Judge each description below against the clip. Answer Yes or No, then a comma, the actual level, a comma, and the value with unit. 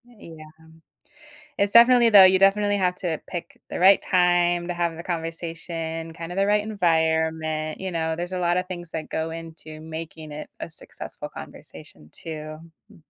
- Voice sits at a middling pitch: Yes, medium, 170 Hz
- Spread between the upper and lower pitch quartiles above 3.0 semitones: No, narrow, 2.5 semitones